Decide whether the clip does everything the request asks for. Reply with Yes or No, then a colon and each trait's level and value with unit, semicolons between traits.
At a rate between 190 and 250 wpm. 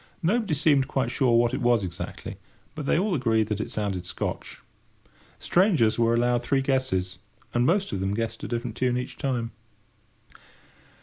No: average, 170 wpm